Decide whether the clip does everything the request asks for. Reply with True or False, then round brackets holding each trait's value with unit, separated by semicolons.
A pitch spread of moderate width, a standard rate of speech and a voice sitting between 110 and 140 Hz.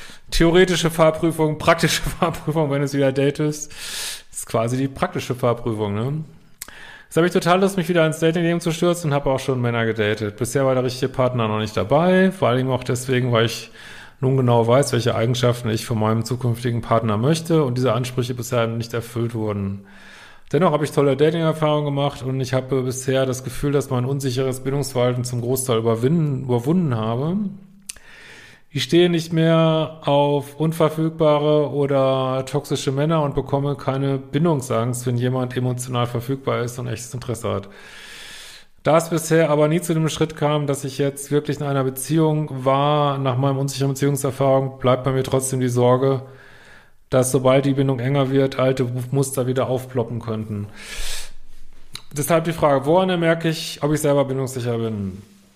True (3.6 semitones; 165 wpm; 135 Hz)